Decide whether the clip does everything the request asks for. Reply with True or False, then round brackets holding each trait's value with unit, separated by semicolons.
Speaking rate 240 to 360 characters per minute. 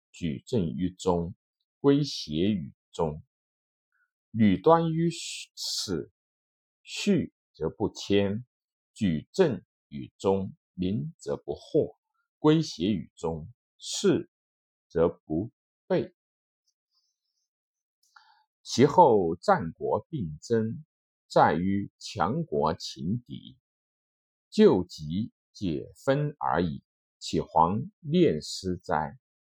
False (110 characters per minute)